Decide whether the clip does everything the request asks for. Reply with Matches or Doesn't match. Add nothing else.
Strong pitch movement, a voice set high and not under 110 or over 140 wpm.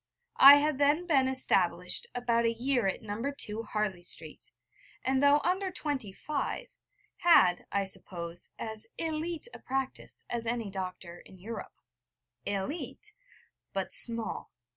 Matches